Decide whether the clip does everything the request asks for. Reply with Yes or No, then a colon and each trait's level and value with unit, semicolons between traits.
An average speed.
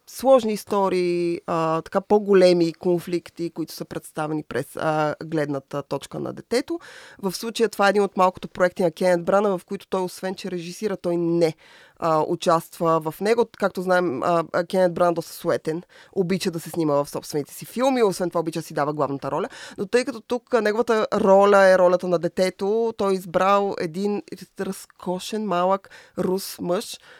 No: fast, 175 wpm